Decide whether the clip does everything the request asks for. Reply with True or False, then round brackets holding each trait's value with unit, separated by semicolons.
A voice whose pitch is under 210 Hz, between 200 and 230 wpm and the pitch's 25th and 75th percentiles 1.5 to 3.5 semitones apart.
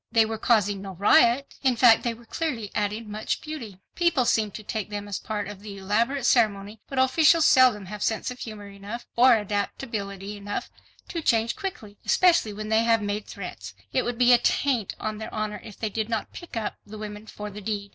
False (215 Hz; 205 wpm; 2.7 semitones)